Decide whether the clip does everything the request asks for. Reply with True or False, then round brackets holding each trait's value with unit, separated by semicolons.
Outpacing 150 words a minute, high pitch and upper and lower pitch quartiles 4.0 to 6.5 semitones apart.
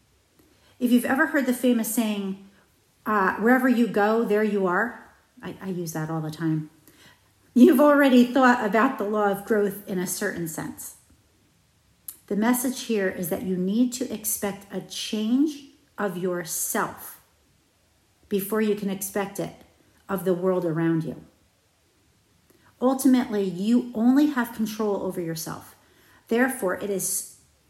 False (145 wpm; 205 Hz; 4.6 semitones)